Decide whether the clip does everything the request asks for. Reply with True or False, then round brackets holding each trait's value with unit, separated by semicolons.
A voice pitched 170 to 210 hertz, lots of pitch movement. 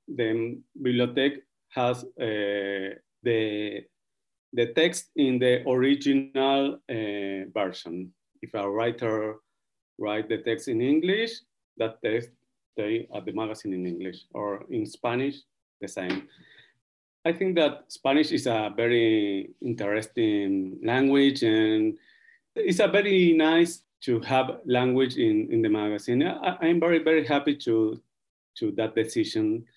False (125 Hz; 6.9 semitones)